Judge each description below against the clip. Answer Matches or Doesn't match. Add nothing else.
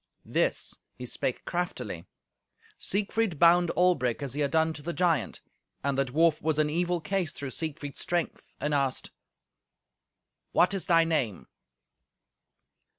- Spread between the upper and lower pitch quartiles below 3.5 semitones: Doesn't match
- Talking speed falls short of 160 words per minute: Matches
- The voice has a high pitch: Doesn't match